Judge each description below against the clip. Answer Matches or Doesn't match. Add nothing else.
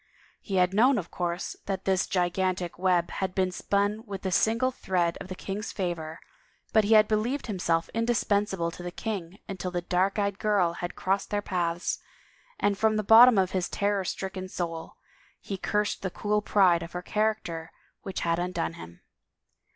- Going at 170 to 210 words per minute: Matches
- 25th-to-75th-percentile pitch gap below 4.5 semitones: Matches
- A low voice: Doesn't match